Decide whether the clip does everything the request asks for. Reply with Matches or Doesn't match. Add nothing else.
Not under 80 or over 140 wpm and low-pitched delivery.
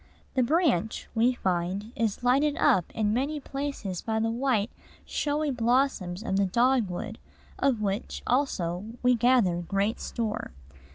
Doesn't match